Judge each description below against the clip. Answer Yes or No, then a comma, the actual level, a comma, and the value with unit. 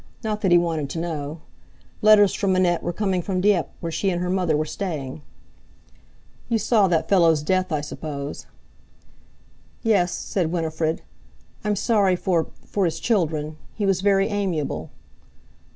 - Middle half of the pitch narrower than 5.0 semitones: Yes, average, 3.7 semitones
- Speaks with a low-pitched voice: No, medium, 175 Hz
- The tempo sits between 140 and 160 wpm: Yes, average, 150 wpm